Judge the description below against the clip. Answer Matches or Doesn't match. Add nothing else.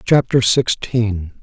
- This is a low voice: Matches